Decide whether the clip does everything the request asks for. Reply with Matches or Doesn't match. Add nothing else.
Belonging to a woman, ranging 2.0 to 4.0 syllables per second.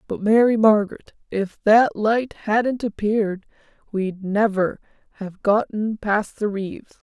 Matches